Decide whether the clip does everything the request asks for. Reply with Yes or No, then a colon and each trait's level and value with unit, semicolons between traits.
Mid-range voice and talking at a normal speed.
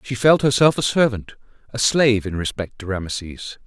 No: low, 115 Hz; average, 180 wpm